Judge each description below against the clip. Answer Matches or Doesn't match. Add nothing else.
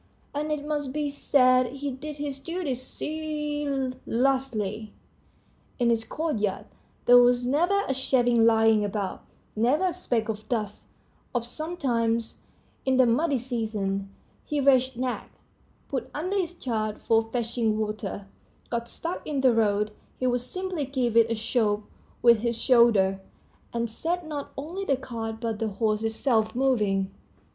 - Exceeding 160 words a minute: Doesn't match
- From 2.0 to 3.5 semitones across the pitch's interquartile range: Doesn't match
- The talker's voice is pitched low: Doesn't match